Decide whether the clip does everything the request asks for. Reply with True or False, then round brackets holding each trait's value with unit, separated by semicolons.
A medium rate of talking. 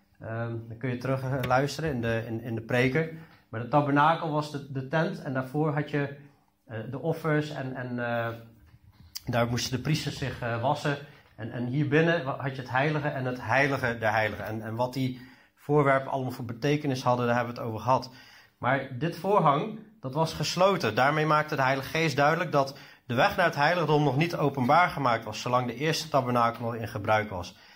False (210 wpm)